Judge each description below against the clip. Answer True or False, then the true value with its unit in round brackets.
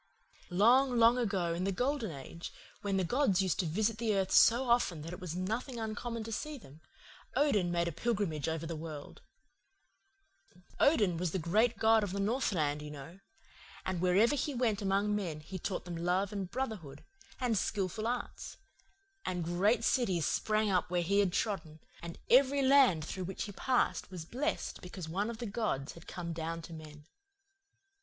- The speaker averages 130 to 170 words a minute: False (180 wpm)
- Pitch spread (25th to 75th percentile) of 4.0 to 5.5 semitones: True (5.1 semitones)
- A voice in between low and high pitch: False (195 Hz)